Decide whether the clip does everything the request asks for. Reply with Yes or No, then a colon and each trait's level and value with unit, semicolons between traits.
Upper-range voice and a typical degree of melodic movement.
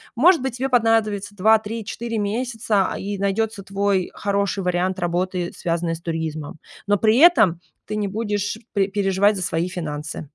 Yes: high, 200 Hz; average, 3.4 semitones